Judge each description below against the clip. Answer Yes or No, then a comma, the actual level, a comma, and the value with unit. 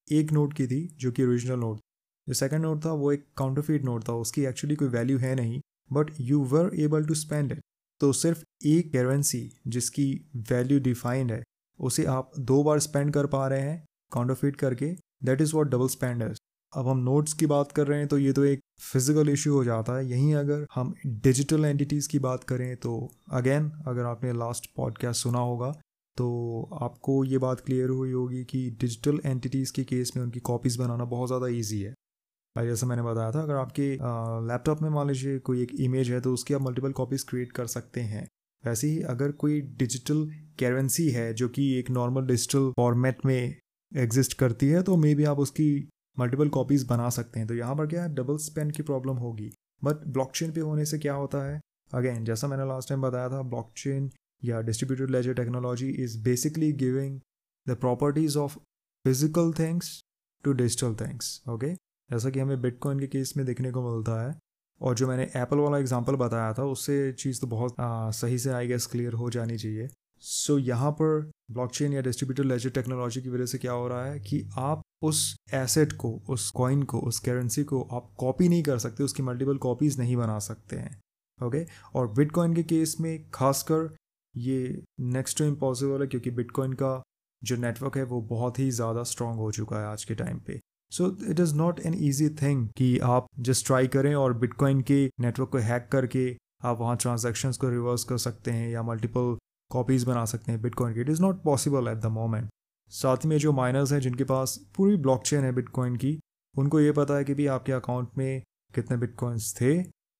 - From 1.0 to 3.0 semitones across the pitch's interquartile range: Yes, average, 2.7 semitones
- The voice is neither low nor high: No, low, 130 Hz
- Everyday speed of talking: No, fast, 200 wpm